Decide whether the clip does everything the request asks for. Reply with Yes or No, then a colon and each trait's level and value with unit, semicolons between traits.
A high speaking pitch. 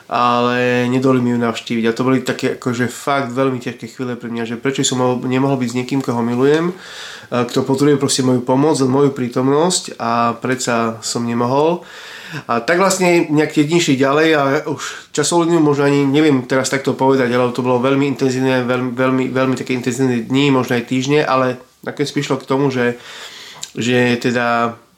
No: low, 130 Hz